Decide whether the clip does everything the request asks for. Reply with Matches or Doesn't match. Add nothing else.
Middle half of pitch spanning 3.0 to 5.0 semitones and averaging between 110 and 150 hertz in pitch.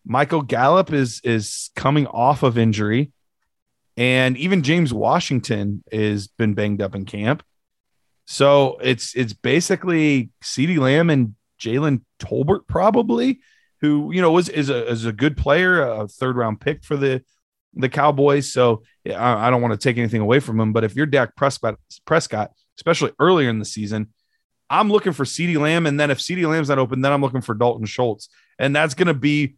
Matches